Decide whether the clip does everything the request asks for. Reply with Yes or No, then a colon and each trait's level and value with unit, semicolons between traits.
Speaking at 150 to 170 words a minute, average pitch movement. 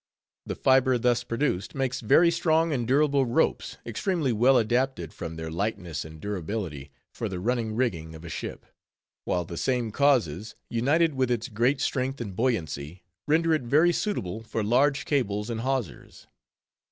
No: average, 160 wpm; wide, 6.0 semitones